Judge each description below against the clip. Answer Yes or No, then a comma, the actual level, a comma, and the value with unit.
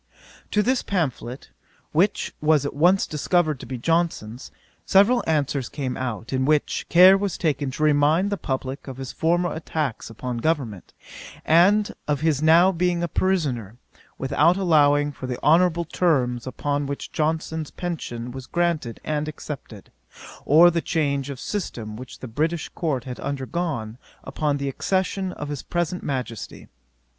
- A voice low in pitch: No, medium, 150 Hz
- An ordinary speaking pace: Yes, average, 150 wpm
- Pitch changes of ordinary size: Yes, average, 4.6 semitones